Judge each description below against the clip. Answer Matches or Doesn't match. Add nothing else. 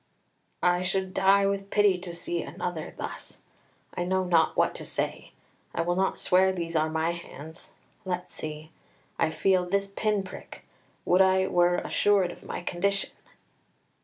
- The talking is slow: Doesn't match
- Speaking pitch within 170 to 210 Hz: Matches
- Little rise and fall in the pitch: Matches